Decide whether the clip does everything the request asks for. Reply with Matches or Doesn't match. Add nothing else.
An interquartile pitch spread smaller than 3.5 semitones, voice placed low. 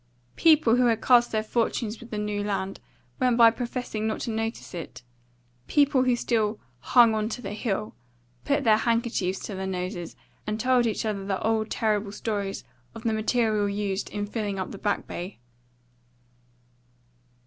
Doesn't match